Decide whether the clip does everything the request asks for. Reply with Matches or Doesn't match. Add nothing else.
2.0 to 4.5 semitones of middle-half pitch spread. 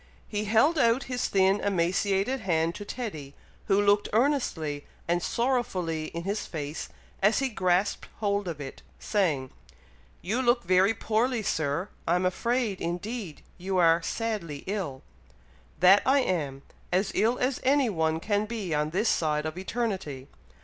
Doesn't match